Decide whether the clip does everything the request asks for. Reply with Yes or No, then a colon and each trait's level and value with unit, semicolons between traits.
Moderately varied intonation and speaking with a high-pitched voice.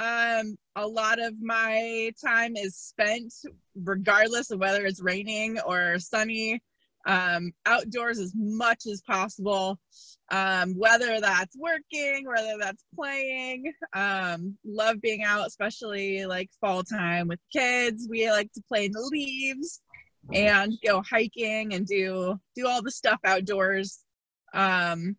Yes: average, 3.0 semitones; high, 215 Hz